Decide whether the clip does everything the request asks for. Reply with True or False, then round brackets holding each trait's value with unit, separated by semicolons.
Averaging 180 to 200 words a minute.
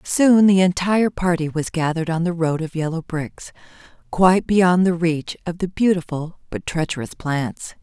False (170 wpm)